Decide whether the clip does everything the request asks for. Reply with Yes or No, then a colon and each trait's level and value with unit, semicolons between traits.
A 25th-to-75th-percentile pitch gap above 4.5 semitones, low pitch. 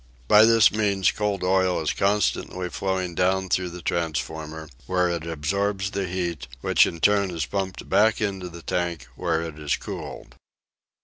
No: average, 2.8 semitones; very low, 90 Hz